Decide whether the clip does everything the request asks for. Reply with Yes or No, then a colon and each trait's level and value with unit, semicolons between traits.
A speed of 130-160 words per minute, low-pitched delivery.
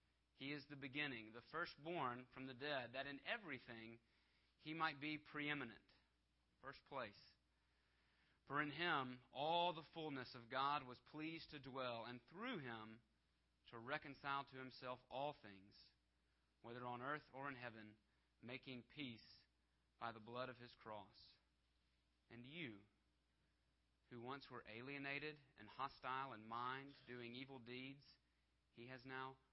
Yes: average, 140 wpm; low, 125 Hz